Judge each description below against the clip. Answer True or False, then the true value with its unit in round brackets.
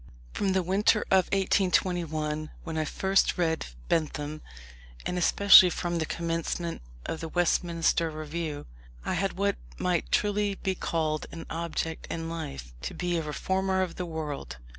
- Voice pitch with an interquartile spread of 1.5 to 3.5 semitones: True (2.9 semitones)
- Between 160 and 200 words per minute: False (150 wpm)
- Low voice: False (170 Hz)